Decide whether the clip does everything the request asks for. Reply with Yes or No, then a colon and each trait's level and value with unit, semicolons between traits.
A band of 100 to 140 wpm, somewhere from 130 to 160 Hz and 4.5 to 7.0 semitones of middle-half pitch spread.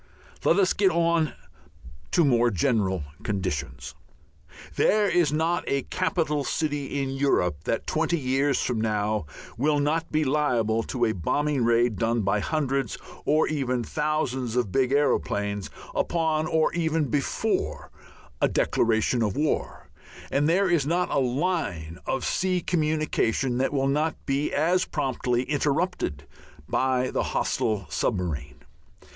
Yes: slow, 135 wpm; low, 135 Hz; average, 5.3 semitones